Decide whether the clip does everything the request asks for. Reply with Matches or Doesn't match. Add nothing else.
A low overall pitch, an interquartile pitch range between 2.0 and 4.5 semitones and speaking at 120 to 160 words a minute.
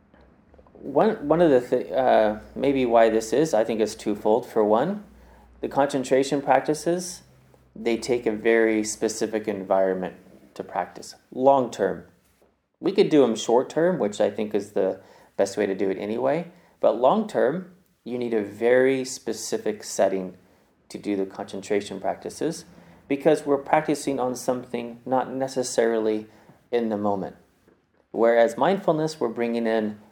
Matches